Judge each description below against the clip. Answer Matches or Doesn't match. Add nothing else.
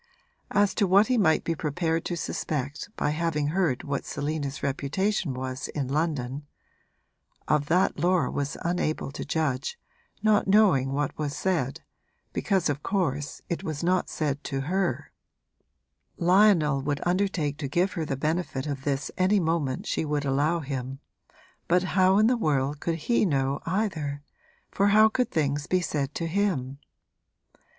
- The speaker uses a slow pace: Doesn't match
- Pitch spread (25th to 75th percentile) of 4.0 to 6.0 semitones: Matches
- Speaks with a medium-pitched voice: Matches